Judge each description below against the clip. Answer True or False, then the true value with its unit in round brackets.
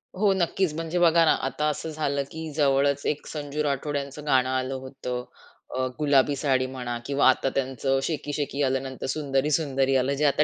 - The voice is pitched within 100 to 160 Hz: True (140 Hz)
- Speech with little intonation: True (2.2 semitones)